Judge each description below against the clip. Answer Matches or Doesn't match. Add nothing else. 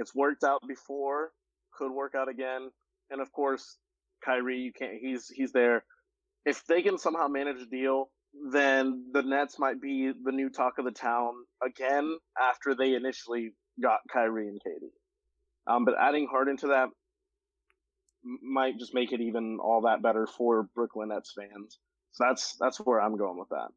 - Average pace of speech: Matches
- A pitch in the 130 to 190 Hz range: Matches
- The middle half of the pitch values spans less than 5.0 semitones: Matches